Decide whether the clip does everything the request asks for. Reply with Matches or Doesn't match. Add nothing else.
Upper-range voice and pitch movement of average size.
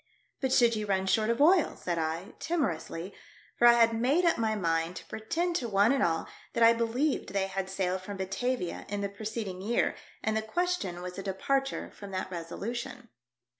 Matches